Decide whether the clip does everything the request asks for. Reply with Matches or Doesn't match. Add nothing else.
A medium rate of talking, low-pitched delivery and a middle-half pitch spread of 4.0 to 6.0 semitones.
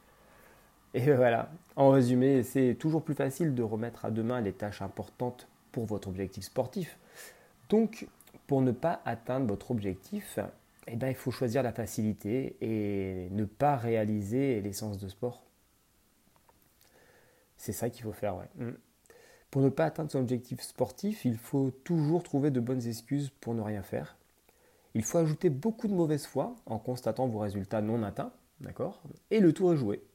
Matches